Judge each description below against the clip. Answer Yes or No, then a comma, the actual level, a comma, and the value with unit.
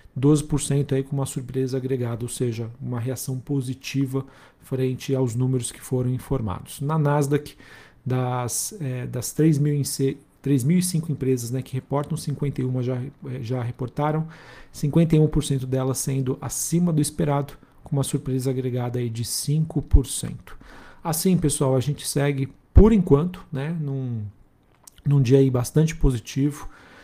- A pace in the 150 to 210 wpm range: No, average, 130 wpm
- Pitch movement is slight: Yes, narrow, 2.2 semitones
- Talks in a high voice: No, low, 135 Hz